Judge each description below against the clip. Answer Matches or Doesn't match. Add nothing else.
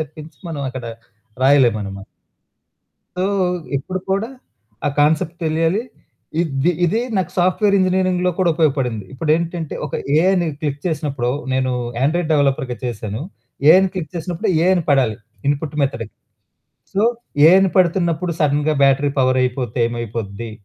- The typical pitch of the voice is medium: Matches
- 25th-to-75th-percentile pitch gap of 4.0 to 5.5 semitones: Matches